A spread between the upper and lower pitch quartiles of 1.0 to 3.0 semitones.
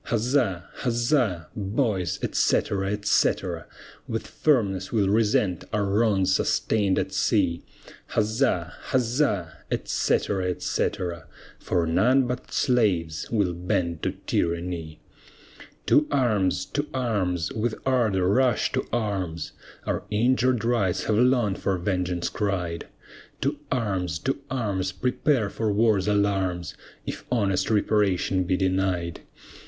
No: average, 4.4 semitones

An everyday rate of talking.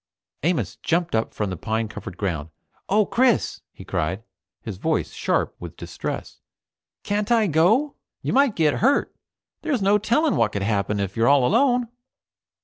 Yes: average, 160 wpm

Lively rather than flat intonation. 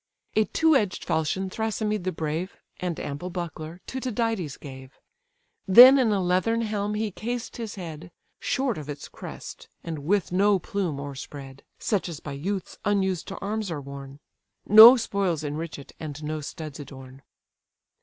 Yes: wide, 5.8 semitones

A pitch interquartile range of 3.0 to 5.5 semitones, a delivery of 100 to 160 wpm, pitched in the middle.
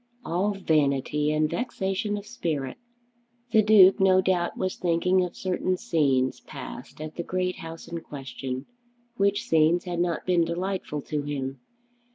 Yes: average, 3.9 semitones; average, 150 wpm; medium, 170 Hz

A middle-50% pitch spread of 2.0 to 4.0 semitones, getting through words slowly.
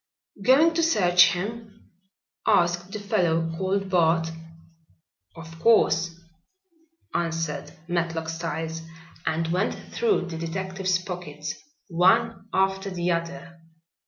Yes: average, 2.8 semitones; slow, 100 wpm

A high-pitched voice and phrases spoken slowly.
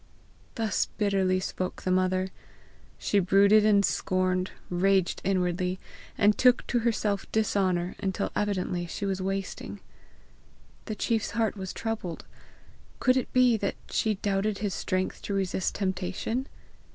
Yes: high, 195 Hz; slow, 130 wpm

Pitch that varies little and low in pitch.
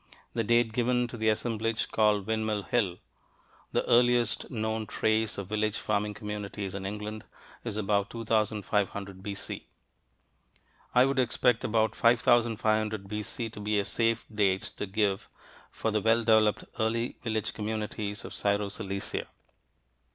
Yes: narrow, 1.8 semitones; low, 110 Hz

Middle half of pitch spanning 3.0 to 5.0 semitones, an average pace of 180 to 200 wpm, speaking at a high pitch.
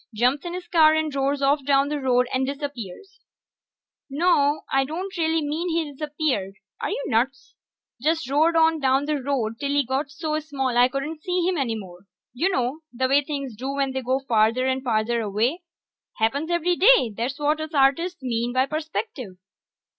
Yes: average, 3.5 semitones; average, 185 wpm; very high, 280 Hz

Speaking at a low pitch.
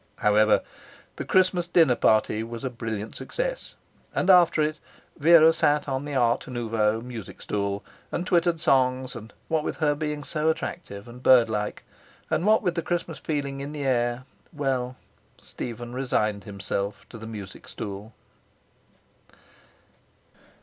Yes: low, 130 Hz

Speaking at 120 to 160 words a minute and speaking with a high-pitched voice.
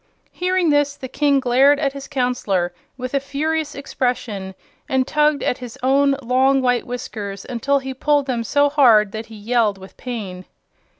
No: average, 170 wpm; very high, 260 Hz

